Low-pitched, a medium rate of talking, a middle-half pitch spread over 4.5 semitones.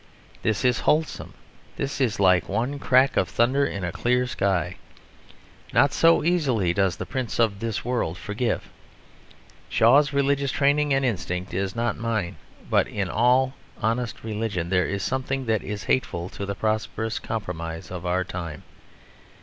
Yes: low, 110 Hz; average, 155 wpm; average, 5.3 semitones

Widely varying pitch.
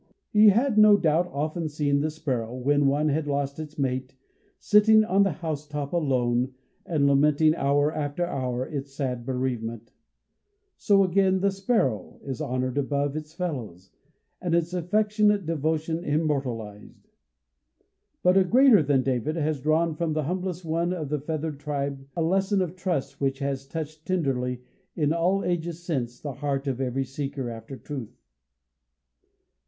No: average, 4.1 semitones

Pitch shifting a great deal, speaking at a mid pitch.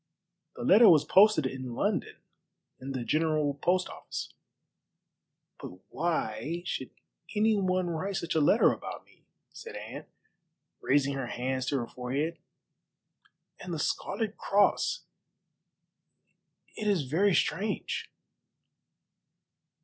Yes: wide, 6.3 semitones; medium, 160 Hz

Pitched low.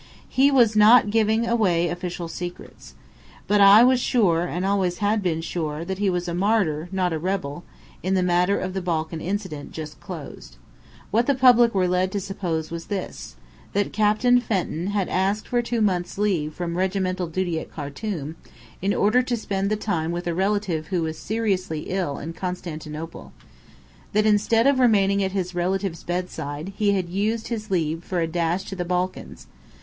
No: medium, 185 Hz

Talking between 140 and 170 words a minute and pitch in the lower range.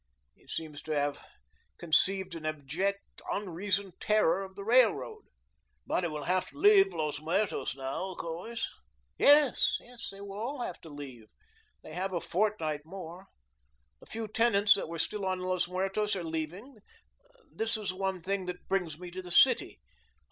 No: average, 165 wpm; medium, 185 Hz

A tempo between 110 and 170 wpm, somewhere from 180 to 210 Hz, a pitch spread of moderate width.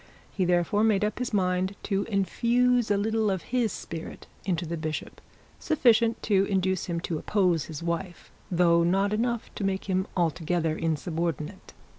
Yes: average, 160 wpm; high, 190 Hz; average, 3.8 semitones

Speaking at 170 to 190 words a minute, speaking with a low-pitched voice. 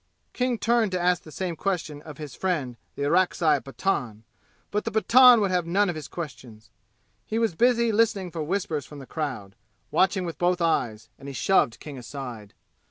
No: average, 185 wpm; medium, 170 Hz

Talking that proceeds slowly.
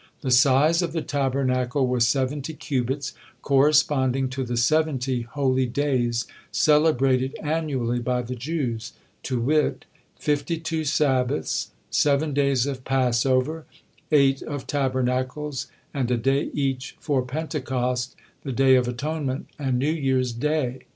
Yes: slow, 130 wpm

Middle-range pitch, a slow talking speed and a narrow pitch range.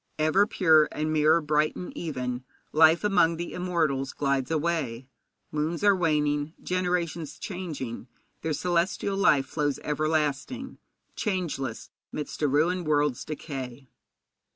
No: medium, 155 Hz; slow, 120 wpm; average, 3.1 semitones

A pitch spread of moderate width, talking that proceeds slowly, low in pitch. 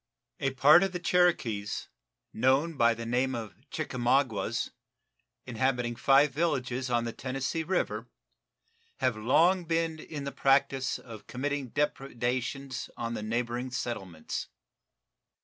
Yes: average, 3.4 semitones; slow, 120 wpm; low, 130 Hz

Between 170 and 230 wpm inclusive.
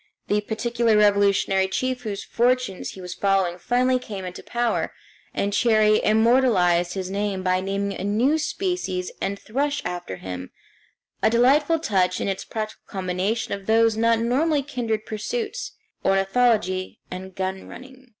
No: average, 150 wpm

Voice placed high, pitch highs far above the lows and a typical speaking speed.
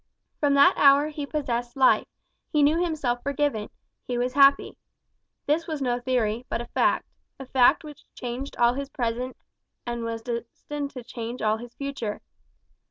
No: very high, 255 Hz; average, 3.0 semitones; average, 165 wpm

